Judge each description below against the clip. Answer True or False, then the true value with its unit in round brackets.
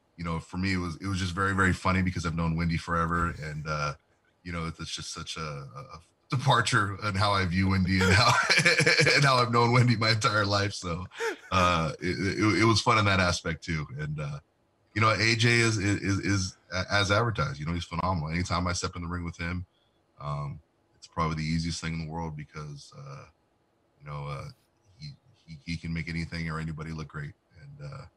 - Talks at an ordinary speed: False (215 wpm)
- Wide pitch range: True (5.7 semitones)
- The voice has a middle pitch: False (95 Hz)